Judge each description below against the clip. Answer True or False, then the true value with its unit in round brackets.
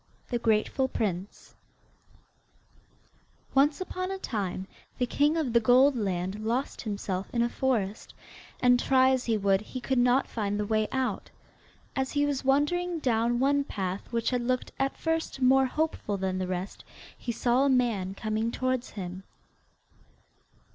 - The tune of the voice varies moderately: True (4.4 semitones)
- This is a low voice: False (245 Hz)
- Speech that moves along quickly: False (155 wpm)